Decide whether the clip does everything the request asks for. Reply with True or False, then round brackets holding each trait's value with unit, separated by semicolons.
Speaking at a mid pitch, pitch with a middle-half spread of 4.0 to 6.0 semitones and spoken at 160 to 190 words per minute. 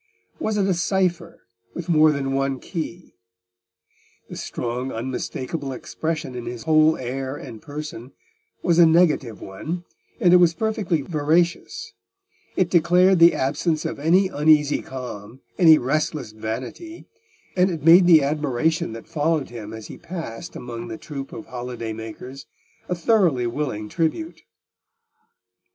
False (155 Hz; 5.2 semitones; 140 wpm)